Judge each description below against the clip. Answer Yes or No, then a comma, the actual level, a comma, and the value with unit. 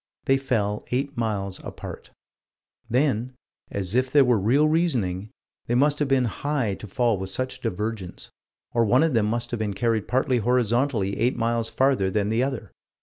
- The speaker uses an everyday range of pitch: Yes, average, 3.8 semitones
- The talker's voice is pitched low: Yes, low, 120 Hz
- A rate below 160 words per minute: No, average, 175 wpm